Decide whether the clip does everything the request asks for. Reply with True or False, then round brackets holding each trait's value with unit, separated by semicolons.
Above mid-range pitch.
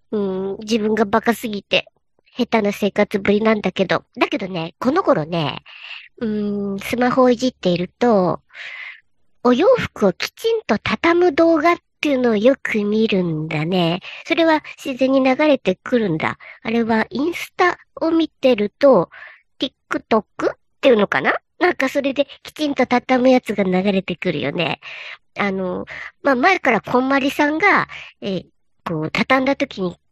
True (240 Hz)